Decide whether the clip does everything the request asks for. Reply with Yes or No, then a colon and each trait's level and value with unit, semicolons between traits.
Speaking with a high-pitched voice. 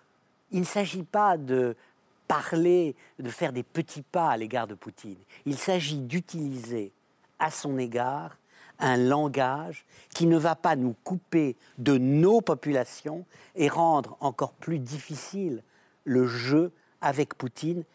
No: medium, 145 Hz